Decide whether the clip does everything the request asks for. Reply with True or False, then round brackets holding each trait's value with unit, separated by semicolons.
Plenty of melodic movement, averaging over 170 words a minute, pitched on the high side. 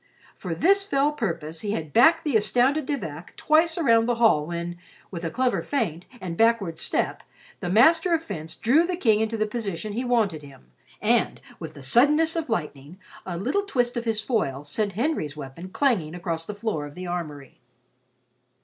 True (8.0 semitones; 185 wpm; 215 Hz)